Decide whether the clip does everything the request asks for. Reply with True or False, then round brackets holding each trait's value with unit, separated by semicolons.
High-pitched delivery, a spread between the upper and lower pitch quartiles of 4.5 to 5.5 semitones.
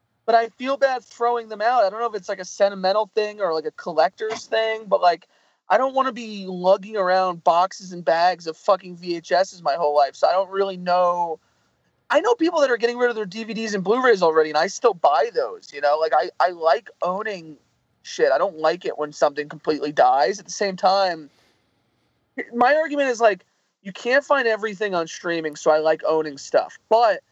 True (195 Hz; 5.1 semitones)